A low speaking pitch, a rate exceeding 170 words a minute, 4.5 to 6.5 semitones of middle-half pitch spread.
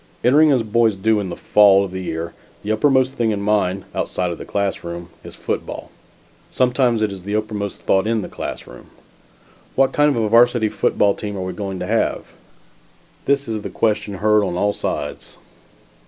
No: low, 105 Hz; average, 185 wpm; average, 3.0 semitones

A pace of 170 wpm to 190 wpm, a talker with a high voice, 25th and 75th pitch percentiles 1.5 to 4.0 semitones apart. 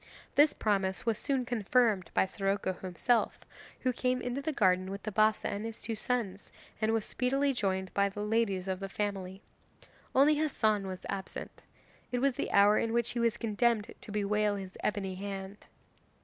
Yes: average, 175 wpm; high, 210 Hz; average, 3.6 semitones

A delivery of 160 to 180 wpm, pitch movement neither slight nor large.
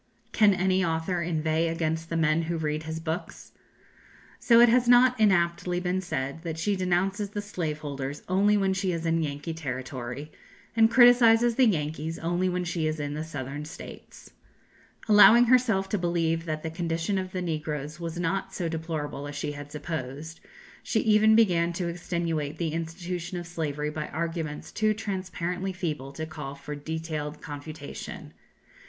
Yes: average, 165 wpm; average, 3.4 semitones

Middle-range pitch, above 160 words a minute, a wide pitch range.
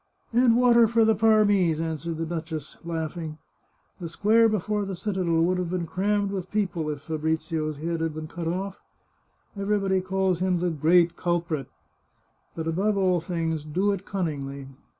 No: medium, 175 Hz; average, 170 wpm; average, 3.6 semitones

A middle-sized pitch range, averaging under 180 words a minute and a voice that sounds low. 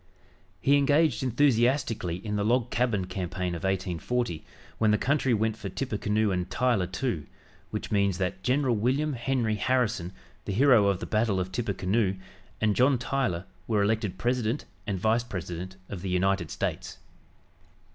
Yes: average, 4.7 semitones; average, 155 wpm; low, 110 Hz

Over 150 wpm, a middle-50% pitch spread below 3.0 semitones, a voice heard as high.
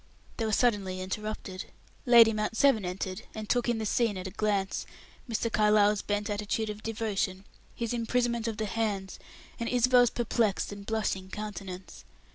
Yes: average, 160 wpm; narrow, 2.5 semitones; high, 215 Hz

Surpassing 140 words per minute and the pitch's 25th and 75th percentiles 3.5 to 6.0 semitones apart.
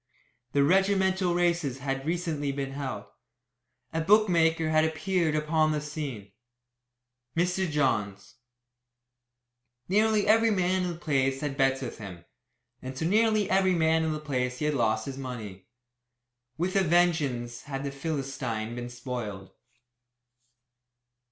No: slow, 135 wpm; average, 5.1 semitones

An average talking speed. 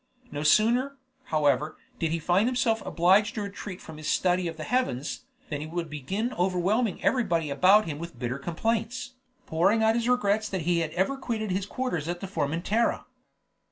Yes: average, 175 wpm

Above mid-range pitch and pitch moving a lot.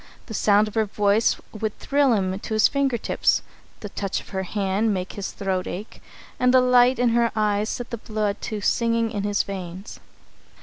No: high, 215 Hz; average, 2.7 semitones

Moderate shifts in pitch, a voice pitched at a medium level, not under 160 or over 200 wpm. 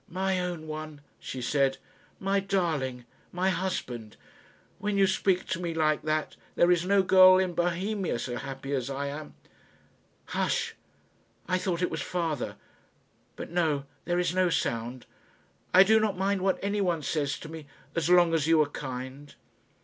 Yes: average, 4.5 semitones; medium, 170 Hz; average, 165 wpm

